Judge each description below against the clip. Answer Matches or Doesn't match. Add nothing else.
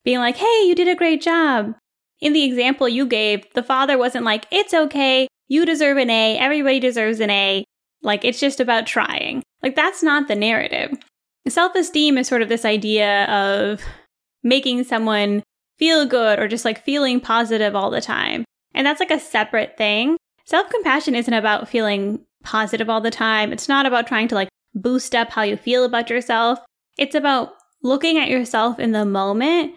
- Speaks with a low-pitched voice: Doesn't match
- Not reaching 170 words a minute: Doesn't match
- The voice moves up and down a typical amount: Matches